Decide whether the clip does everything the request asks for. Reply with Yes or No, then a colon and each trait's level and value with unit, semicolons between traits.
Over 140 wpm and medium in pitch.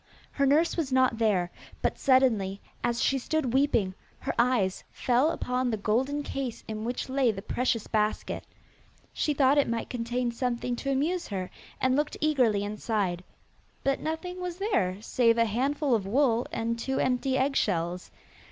No: average, 160 wpm; very high, 250 Hz